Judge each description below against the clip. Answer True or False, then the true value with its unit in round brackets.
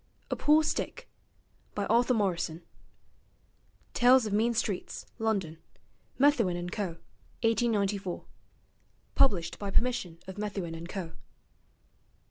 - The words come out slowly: True (105 wpm)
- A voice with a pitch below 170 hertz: False (205 Hz)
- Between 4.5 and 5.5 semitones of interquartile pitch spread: True (4.9 semitones)